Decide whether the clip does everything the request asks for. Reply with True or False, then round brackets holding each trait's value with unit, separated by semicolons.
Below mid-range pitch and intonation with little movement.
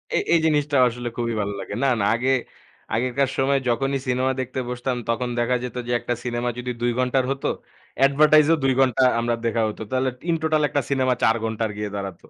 True (125 Hz; 2.3 semitones)